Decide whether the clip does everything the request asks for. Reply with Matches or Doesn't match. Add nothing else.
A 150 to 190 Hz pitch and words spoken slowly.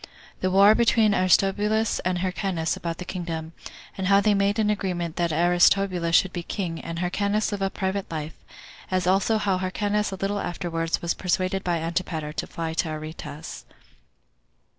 Doesn't match